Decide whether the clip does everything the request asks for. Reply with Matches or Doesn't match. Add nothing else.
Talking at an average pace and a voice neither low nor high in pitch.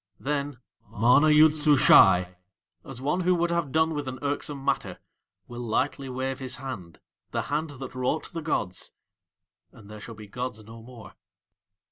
Doesn't match